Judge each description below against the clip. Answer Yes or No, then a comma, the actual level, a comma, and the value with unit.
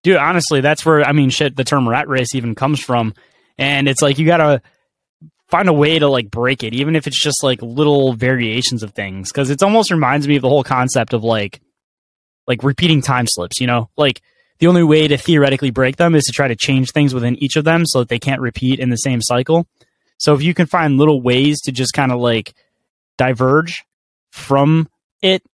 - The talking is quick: Yes, fast, 225 wpm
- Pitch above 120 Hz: Yes, medium, 140 Hz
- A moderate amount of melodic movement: Yes, average, 3.3 semitones